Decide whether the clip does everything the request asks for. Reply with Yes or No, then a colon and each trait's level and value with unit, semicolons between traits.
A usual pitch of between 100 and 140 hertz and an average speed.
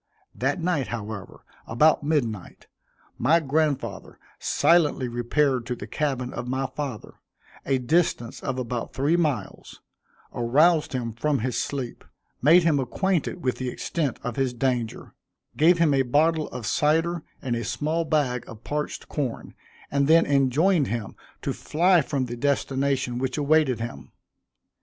Yes: low, 135 Hz; average, 145 wpm